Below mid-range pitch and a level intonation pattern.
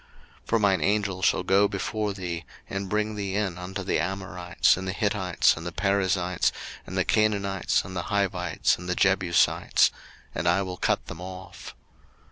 Yes: very low, 95 Hz; narrow, 1.9 semitones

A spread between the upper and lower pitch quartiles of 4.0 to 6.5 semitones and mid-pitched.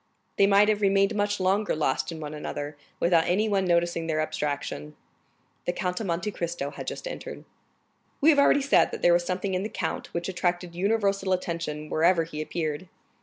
No: average, 3.5 semitones; medium, 175 Hz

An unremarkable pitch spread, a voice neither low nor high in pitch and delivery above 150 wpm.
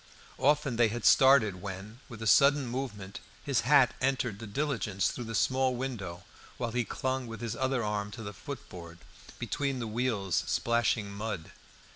No: average, 4.3 semitones; low, 115 Hz; average, 165 wpm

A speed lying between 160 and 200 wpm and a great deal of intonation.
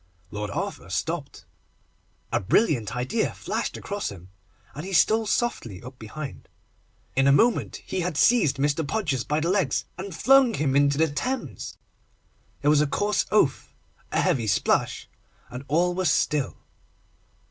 No: average, 150 wpm; wide, 6.7 semitones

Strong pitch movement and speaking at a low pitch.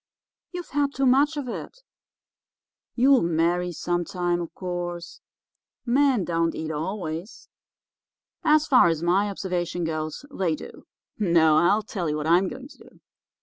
No: wide, 7.0 semitones; medium, 180 Hz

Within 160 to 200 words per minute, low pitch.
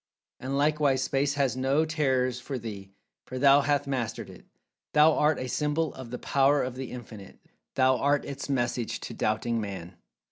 Yes: average, 170 wpm; low, 130 Hz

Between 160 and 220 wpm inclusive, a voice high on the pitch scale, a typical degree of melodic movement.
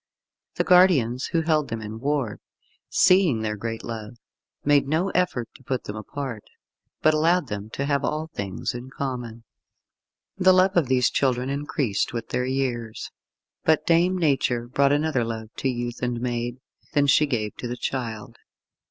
No: average, 165 wpm; low, 130 Hz; average, 4.5 semitones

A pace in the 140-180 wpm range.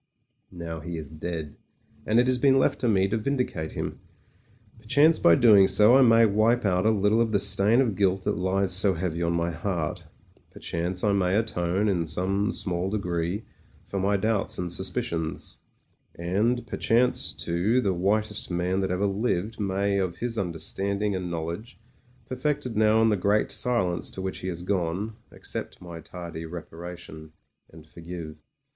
Yes: average, 175 wpm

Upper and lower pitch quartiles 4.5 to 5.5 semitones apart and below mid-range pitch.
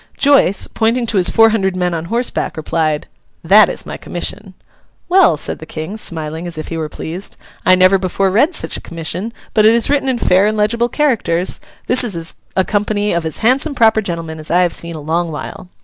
No: average, 5.1 semitones; high, 190 Hz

